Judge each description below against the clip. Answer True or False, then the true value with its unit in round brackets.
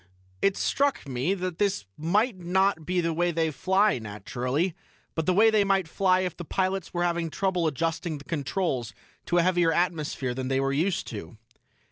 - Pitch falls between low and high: True (175 Hz)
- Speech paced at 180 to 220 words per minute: True (185 wpm)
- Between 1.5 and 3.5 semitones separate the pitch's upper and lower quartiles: False (4.1 semitones)